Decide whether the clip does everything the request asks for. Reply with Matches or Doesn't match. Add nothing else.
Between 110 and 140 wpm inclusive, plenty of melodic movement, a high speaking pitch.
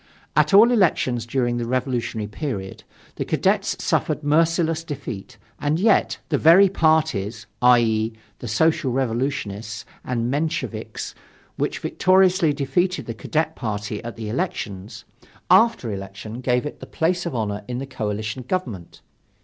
Doesn't match